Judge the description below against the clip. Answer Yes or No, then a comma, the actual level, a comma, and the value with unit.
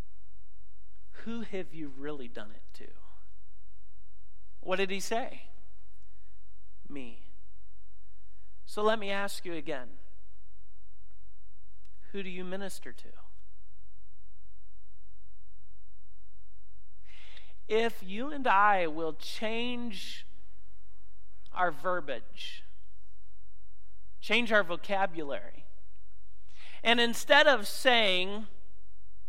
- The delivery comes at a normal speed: No, slow, 80 wpm